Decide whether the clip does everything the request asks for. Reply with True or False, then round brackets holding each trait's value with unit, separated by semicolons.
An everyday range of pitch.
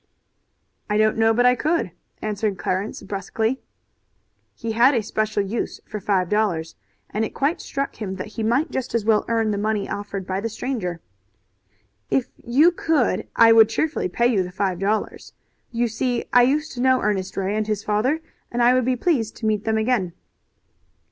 True (3.2 semitones)